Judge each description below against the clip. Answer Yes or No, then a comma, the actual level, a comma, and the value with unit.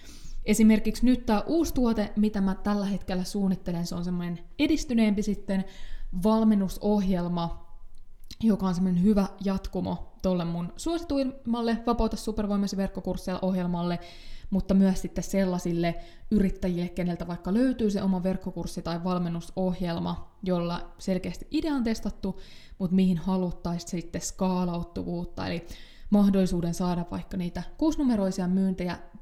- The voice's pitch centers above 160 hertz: Yes, high, 190 Hz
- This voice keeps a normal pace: Yes, average, 120 wpm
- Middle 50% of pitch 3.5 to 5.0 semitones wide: No, average, 3.0 semitones